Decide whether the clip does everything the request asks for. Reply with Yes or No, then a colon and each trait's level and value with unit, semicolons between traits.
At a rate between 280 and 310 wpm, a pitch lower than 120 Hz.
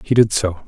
No: fast, 265 wpm; low, 105 Hz